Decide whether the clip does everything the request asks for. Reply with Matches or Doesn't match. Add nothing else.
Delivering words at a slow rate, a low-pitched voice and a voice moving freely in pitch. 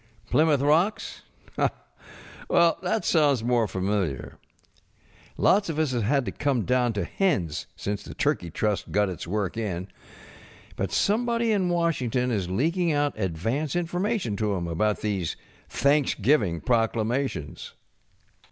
Matches